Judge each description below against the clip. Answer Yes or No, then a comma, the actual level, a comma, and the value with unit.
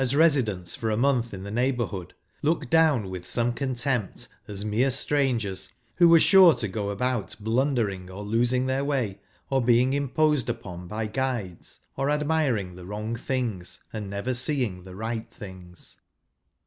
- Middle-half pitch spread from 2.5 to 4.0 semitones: No, average, 5.0 semitones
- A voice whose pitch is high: No, low, 120 Hz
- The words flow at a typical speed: Yes, average, 165 wpm